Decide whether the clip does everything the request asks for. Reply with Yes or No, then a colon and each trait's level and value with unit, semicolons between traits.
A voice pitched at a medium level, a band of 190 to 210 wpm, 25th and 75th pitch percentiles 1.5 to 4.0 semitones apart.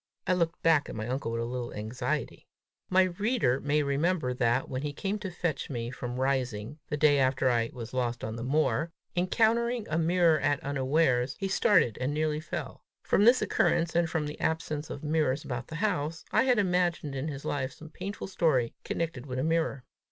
No: medium, 150 Hz; average, 200 wpm; average, 4.8 semitones